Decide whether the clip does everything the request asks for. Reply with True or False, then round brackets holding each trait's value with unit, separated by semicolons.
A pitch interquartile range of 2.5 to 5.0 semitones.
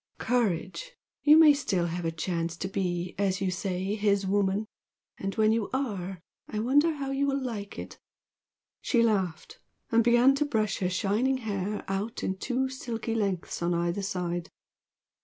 True (4.7 semitones)